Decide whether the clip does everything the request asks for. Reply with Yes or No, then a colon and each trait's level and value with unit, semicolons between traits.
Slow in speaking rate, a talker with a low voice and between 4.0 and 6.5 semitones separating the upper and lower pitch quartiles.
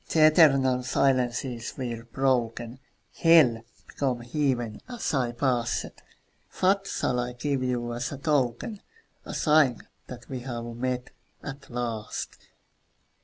No: slow, 120 wpm; low, 125 Hz; average, 2.7 semitones